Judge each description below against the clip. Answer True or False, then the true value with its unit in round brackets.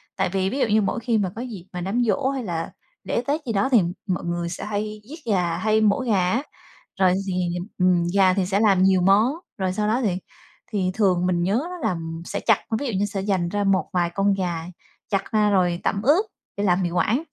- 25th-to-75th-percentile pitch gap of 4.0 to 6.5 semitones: False (3.0 semitones)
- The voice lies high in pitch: True (195 Hz)